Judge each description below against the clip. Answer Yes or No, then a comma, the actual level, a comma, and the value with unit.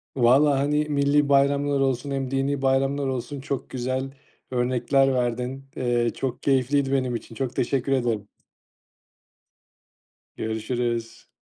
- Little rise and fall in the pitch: Yes, narrow, 2.2 semitones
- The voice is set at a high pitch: No, low, 135 Hz